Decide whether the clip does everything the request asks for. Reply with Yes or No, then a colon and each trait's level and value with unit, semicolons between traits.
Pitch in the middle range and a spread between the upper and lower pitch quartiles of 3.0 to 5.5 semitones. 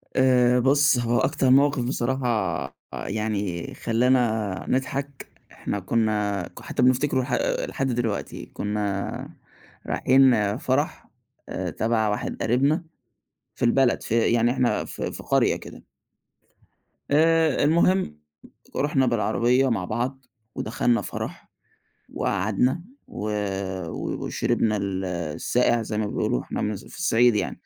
No: low, 120 Hz; average, 3.8 semitones